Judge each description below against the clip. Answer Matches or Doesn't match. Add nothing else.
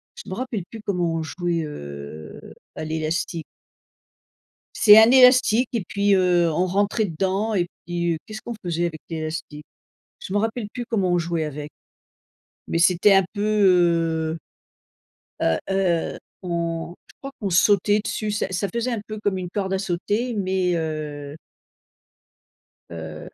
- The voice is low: Doesn't match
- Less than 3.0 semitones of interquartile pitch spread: Doesn't match